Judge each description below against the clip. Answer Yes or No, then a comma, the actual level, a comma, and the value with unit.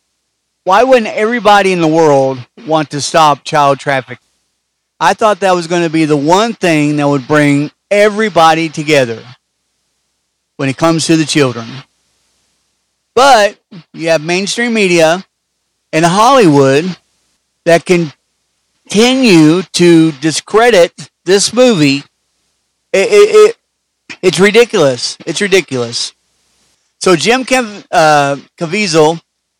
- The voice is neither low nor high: Yes, medium, 165 Hz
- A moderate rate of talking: No, slow, 120 wpm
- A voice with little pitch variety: No, wide, 5.5 semitones